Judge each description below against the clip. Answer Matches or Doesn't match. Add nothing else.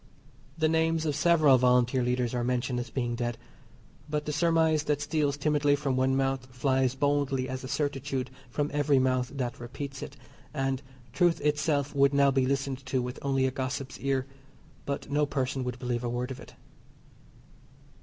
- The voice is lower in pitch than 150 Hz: Matches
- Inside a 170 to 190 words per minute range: Matches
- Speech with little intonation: Matches